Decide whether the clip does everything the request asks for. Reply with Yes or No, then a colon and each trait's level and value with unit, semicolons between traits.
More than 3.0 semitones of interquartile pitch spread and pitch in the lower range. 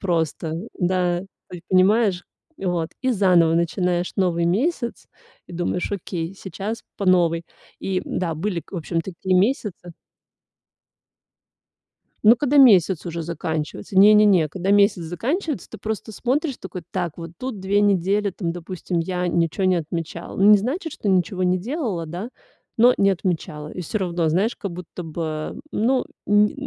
No: average, 3.5 semitones; medium, 185 Hz